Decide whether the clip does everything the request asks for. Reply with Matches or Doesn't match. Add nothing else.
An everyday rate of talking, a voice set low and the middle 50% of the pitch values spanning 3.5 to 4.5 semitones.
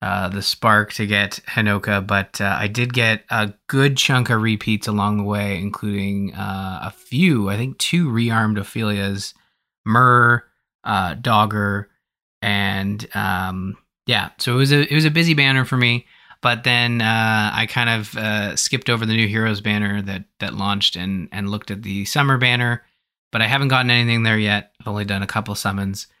Doesn't match